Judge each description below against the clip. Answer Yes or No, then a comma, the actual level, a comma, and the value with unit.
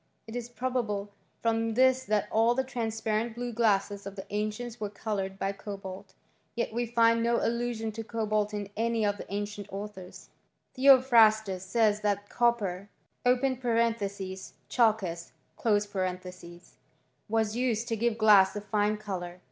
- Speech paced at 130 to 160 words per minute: Yes, average, 140 wpm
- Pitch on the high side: Yes, high, 215 Hz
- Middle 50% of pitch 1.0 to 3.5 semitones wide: Yes, narrow, 2.6 semitones